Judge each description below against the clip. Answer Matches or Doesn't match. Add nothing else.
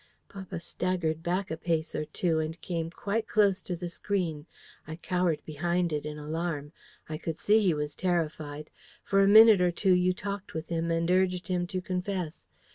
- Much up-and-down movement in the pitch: Doesn't match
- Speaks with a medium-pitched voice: Matches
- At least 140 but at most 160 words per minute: Doesn't match